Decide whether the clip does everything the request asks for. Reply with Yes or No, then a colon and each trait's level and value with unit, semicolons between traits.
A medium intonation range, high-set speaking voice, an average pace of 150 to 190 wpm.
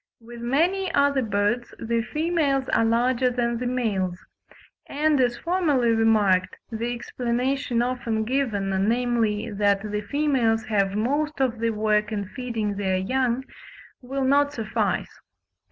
No: average, 3.7 semitones; high, 235 Hz; slow, 135 wpm